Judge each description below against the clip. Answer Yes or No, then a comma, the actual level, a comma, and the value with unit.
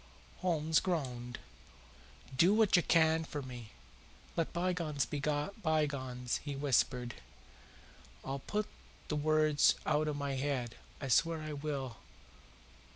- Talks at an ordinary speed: No, slow, 120 wpm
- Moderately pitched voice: Yes, medium, 150 Hz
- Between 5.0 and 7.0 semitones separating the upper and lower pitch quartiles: No, average, 3.2 semitones